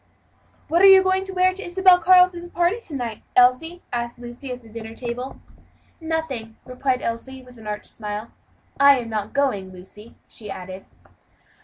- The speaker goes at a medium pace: Yes, average, 170 wpm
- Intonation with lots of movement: Yes, wide, 7.4 semitones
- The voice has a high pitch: Yes, very high, 255 Hz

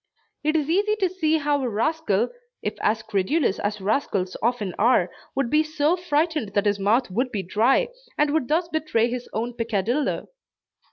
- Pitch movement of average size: No, wide, 6.7 semitones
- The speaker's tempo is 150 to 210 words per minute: Yes, average, 175 wpm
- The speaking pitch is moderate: No, very high, 250 Hz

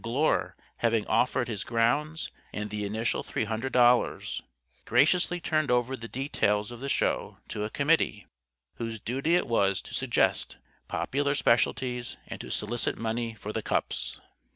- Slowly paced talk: No, average, 155 wpm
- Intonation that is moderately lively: Yes, average, 3.5 semitones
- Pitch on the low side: Yes, low, 120 Hz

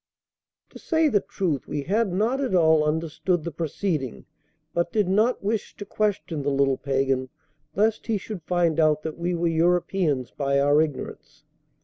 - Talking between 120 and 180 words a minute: Yes, average, 165 wpm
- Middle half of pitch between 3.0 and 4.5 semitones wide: No, average, 5.2 semitones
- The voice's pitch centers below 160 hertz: No, medium, 170 Hz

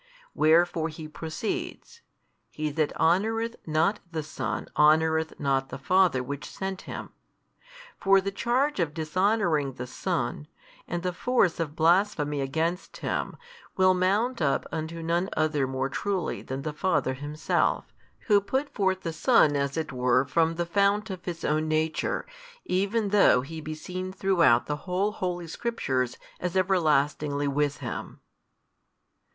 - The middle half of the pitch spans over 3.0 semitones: Yes, average, 4.3 semitones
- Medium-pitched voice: Yes, medium, 165 Hz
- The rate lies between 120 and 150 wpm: Yes, average, 145 wpm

